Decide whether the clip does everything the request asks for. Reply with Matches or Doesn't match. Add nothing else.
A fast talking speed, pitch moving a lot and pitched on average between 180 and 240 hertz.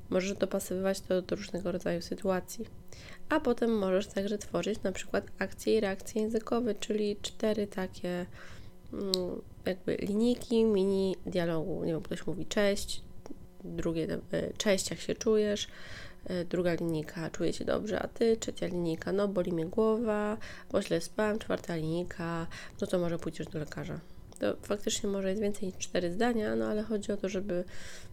Doesn't match